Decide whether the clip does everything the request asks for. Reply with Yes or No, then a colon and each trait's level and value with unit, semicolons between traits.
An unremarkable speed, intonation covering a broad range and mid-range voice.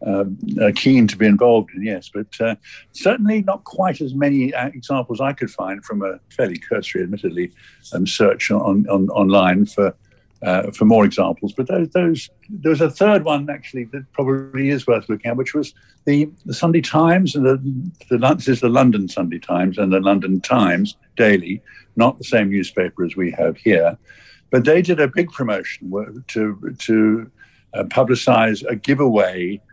No: average, 180 wpm; wide, 6.2 semitones; low, 130 Hz